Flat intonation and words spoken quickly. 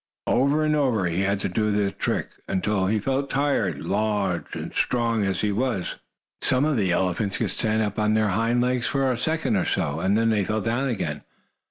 No: average, 4.3 semitones; fast, 210 wpm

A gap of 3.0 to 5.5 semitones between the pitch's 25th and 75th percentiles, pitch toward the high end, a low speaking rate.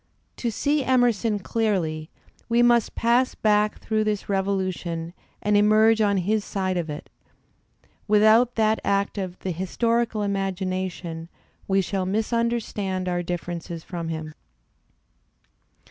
Yes: average, 3.4 semitones; high, 200 Hz; slow, 125 wpm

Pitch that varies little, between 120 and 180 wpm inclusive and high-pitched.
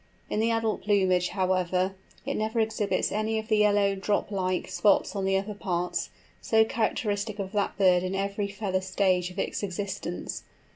Yes: narrow, 2.1 semitones; average, 175 wpm; high, 200 Hz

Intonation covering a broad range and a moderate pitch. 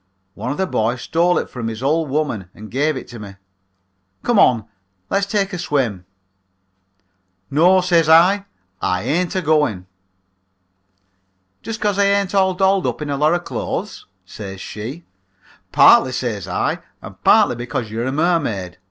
Yes: wide, 7.9 semitones; medium, 150 Hz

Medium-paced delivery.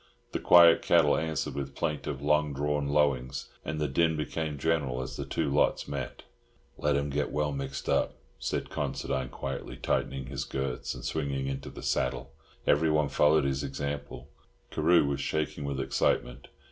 Yes: average, 160 wpm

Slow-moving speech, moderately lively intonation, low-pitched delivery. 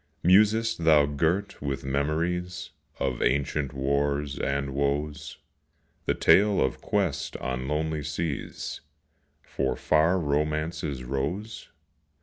Yes: slow, 105 wpm; average, 3.3 semitones; very low, 75 Hz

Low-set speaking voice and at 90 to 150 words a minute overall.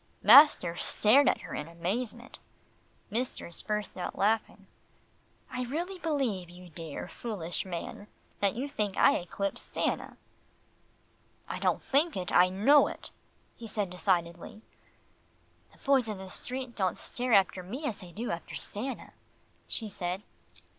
No: high, 210 Hz; average, 140 wpm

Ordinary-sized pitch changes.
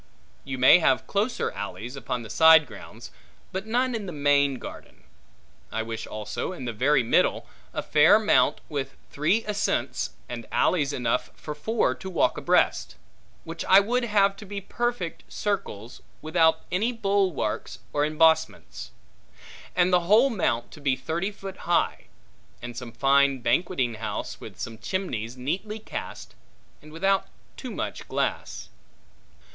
No: wide, 7.2 semitones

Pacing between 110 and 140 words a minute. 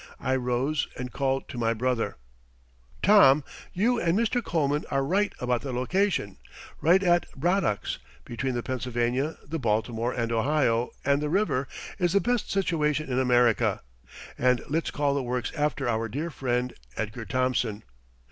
No: average, 155 wpm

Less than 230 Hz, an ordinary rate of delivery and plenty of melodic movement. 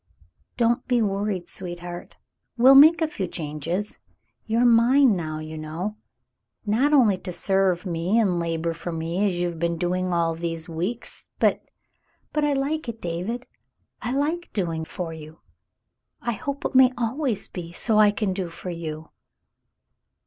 Yes: high, 190 Hz; average, 170 wpm; wide, 5.8 semitones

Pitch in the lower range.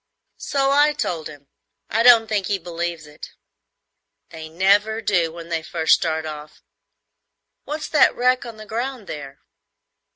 No: medium, 185 Hz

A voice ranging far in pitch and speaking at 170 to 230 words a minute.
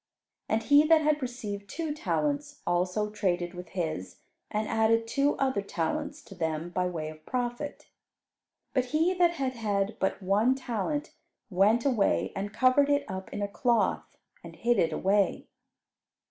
No: wide, 6.6 semitones; average, 160 wpm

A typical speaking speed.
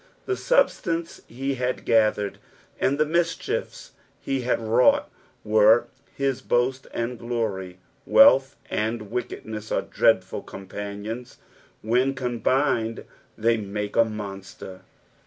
No: slow, 110 wpm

